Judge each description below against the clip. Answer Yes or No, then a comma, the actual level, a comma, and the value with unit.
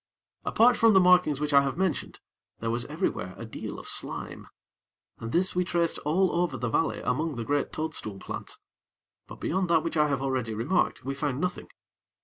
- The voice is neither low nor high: Yes, medium, 150 Hz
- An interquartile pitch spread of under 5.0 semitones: No, wide, 5.5 semitones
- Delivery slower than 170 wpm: No, average, 190 wpm